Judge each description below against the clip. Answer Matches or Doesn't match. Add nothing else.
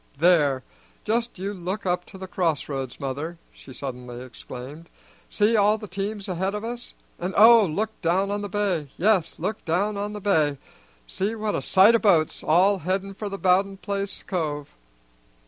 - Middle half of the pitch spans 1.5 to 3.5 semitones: Doesn't match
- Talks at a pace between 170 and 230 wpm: Matches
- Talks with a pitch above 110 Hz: Matches